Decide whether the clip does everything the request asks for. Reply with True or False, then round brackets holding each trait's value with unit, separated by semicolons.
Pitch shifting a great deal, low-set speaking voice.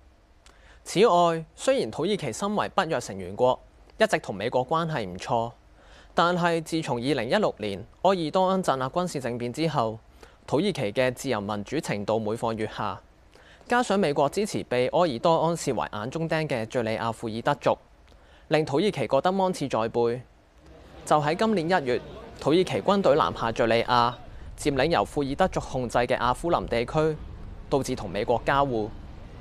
True (6.7 semitones; 125 Hz)